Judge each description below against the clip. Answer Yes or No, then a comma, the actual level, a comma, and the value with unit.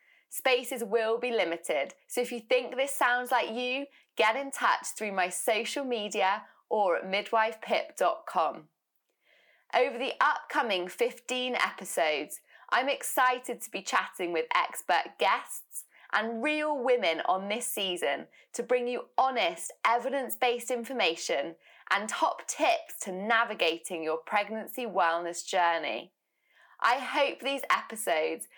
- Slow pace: Yes, slow, 130 wpm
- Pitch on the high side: Yes, high, 240 Hz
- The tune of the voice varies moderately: Yes, average, 4.5 semitones